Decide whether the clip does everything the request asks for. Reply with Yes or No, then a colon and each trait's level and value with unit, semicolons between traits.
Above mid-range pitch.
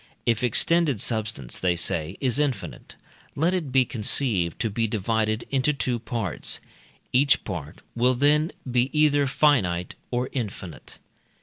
No: low, 120 Hz